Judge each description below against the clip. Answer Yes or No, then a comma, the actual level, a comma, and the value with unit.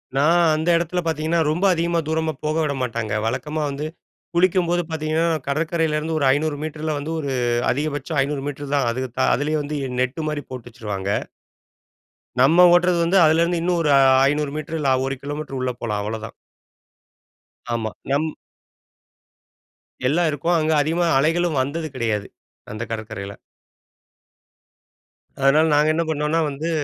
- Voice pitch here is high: No, medium, 150 Hz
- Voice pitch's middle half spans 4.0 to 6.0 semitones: No, average, 3.2 semitones